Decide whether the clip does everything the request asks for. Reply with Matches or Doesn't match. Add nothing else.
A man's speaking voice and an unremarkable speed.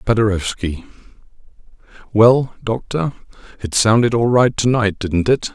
Doesn't match